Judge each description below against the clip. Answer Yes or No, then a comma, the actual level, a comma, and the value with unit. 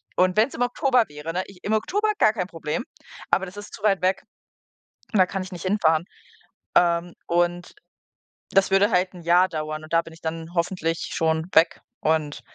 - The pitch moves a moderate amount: Yes, average, 3.1 semitones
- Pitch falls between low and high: Yes, medium, 180 Hz